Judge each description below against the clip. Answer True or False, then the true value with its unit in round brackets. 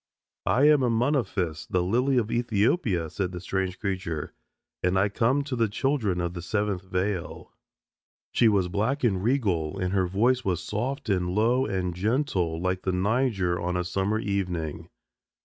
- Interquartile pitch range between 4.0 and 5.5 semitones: True (4.7 semitones)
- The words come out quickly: False (165 wpm)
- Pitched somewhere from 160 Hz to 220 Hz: False (100 Hz)